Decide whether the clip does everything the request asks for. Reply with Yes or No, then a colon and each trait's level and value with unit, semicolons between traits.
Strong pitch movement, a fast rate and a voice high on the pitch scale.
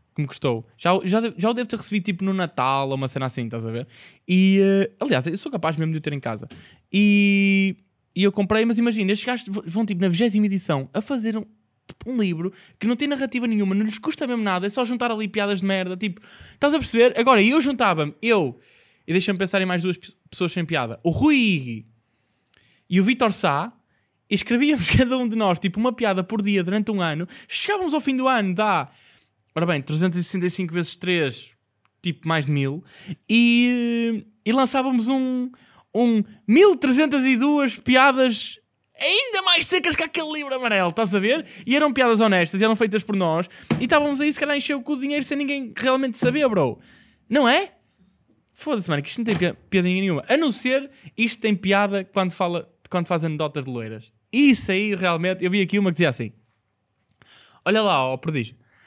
Yes: wide, 6.2 semitones; fast, 200 wpm; high, 200 Hz